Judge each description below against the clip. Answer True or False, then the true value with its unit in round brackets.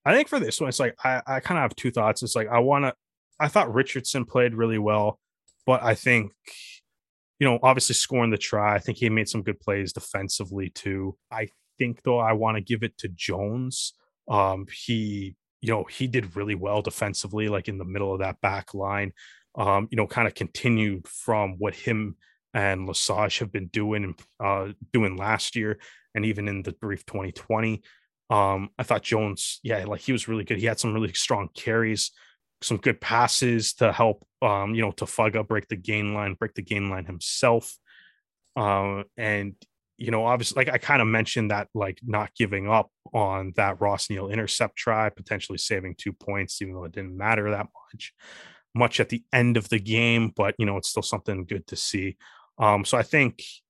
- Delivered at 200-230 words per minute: True (205 wpm)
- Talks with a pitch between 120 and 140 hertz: False (105 Hz)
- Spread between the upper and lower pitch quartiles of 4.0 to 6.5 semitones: False (2.8 semitones)